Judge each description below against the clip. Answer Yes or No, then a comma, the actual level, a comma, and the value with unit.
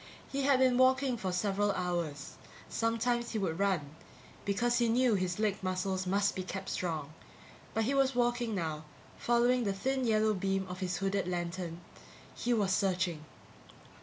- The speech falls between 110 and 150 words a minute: No, average, 165 wpm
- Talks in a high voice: Yes, high, 200 Hz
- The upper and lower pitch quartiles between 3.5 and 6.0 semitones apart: Yes, average, 4.7 semitones